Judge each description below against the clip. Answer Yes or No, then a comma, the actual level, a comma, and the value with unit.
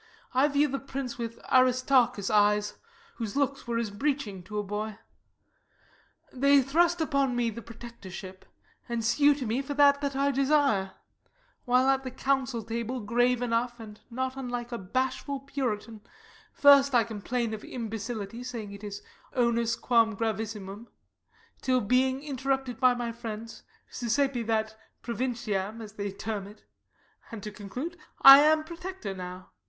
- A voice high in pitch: Yes, high, 240 Hz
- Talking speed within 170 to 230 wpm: No, average, 150 wpm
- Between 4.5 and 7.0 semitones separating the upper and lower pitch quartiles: No, average, 3.8 semitones